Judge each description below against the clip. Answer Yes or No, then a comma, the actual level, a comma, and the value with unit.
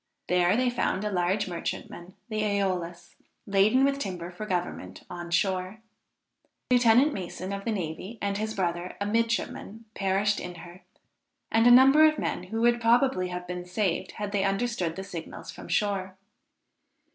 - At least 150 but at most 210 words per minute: Yes, average, 160 wpm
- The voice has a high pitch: Yes, high, 195 Hz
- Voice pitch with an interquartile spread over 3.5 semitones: Yes, average, 3.9 semitones